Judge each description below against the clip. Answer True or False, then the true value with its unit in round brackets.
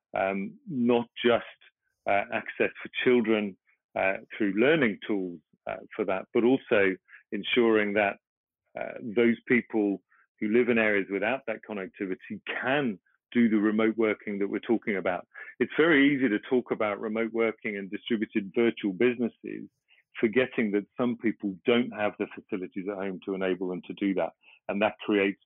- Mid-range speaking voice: False (110 Hz)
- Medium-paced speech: True (160 wpm)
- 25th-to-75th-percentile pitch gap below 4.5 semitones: True (3.1 semitones)